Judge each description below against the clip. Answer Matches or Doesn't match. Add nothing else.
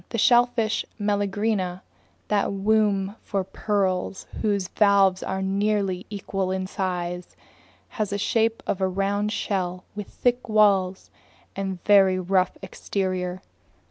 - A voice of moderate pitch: Doesn't match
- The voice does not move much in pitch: Matches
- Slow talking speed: Matches